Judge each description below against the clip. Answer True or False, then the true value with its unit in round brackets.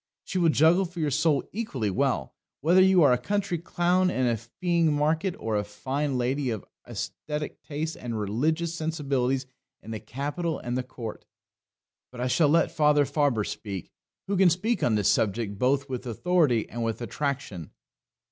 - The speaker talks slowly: False (175 wpm)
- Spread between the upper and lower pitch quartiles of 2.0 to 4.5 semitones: False (5.6 semitones)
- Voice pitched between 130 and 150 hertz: True (140 Hz)